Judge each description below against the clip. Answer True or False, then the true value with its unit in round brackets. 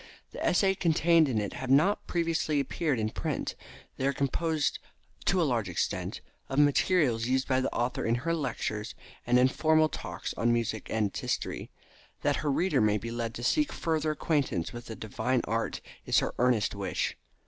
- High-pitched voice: False (130 Hz)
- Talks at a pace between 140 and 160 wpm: False (180 wpm)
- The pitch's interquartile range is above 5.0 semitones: True (5.4 semitones)